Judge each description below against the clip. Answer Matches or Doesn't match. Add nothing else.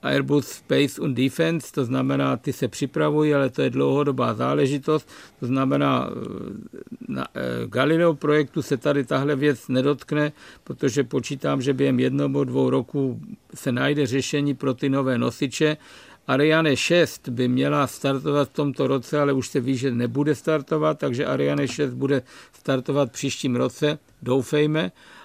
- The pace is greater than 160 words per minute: Doesn't match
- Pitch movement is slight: Matches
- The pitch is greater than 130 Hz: Matches